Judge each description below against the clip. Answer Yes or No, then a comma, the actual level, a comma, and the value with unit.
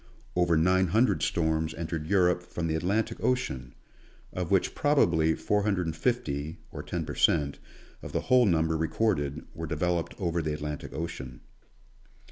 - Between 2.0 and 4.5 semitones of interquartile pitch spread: Yes, average, 3.1 semitones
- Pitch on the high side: No, very low, 85 Hz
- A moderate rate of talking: Yes, average, 155 wpm